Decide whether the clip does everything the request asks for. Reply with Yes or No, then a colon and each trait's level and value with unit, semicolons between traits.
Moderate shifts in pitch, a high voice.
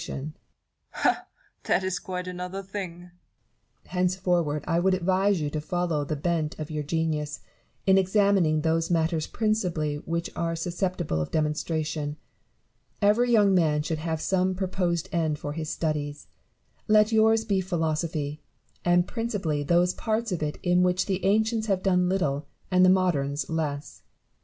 No: average, 3.5 semitones; medium, 175 Hz